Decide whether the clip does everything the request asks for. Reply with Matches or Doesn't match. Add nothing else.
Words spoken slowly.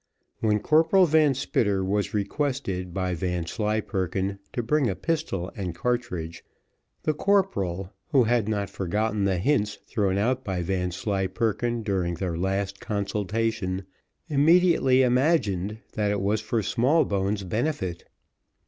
Matches